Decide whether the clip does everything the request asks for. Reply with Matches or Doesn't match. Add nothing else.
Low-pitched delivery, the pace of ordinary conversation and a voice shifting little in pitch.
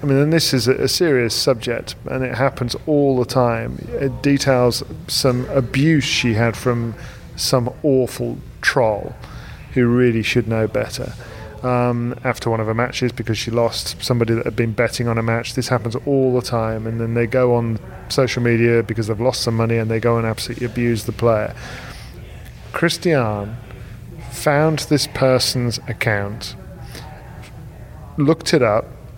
Matches